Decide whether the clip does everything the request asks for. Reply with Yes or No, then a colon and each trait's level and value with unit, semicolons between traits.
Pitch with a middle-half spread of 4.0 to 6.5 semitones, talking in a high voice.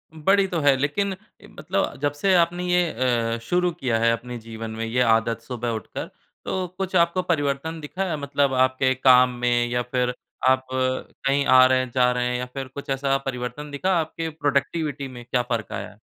No: average, 4.5 semitones; low, 135 Hz